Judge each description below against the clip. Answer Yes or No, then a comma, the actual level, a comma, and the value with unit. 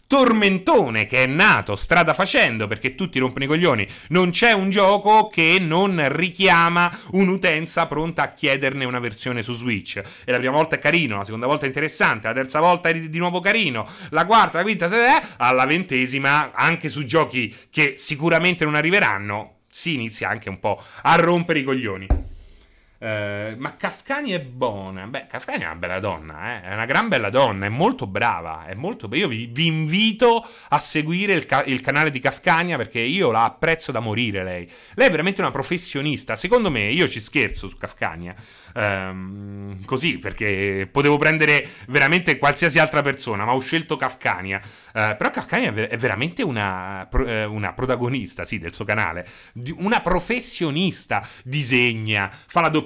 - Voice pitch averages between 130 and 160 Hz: Yes, low, 135 Hz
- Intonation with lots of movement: Yes, wide, 7.3 semitones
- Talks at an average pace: No, fast, 180 wpm